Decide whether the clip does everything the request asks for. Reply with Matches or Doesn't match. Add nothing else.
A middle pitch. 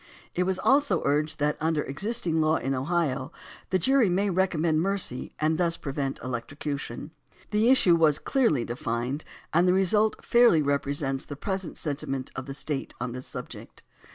Matches